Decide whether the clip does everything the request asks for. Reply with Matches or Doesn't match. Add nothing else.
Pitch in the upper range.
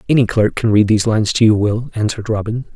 Doesn't match